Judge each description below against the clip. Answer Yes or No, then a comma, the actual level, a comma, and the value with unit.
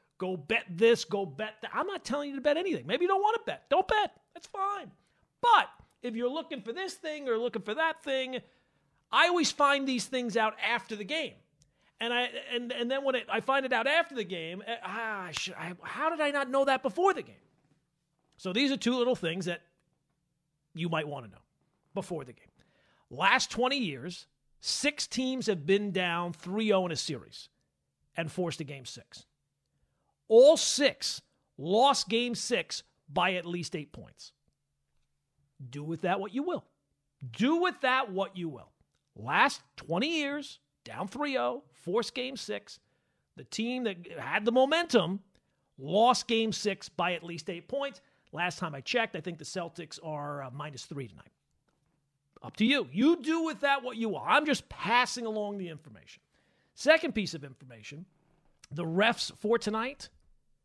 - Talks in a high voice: Yes, high, 210 Hz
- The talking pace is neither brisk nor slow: Yes, average, 180 wpm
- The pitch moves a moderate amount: No, wide, 7.9 semitones